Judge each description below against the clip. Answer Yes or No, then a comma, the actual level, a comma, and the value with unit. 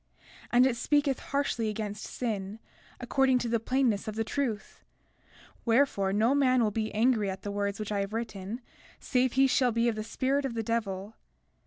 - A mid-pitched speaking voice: No, high, 230 Hz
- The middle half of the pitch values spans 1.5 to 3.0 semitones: No, average, 3.5 semitones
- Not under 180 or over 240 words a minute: Yes, average, 190 wpm